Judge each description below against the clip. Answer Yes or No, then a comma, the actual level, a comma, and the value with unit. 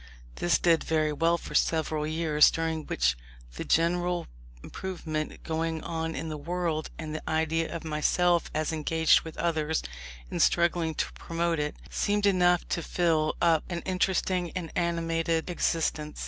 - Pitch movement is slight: Yes, narrow, 1.6 semitones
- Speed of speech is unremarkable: Yes, average, 150 wpm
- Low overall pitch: No, medium, 165 Hz